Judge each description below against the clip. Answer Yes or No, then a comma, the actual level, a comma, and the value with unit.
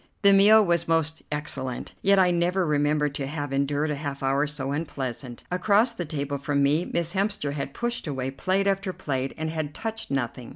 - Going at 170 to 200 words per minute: Yes, average, 195 wpm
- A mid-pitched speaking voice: Yes, medium, 150 Hz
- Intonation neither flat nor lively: Yes, average, 4.7 semitones